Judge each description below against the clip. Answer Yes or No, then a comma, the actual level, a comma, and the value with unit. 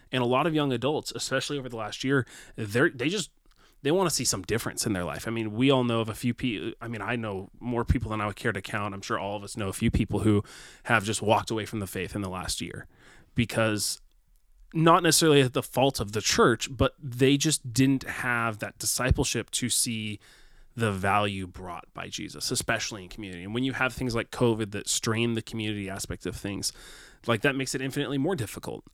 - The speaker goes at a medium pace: No, fast, 230 wpm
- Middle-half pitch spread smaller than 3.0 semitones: No, average, 3.8 semitones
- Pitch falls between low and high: No, low, 115 Hz